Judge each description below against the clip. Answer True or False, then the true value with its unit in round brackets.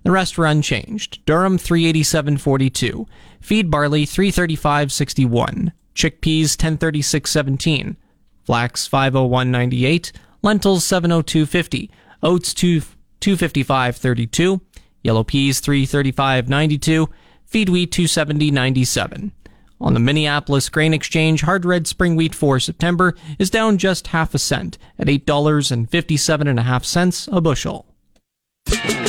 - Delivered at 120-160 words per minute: True (145 wpm)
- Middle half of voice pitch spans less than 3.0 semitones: False (4.1 semitones)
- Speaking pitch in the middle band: True (155 Hz)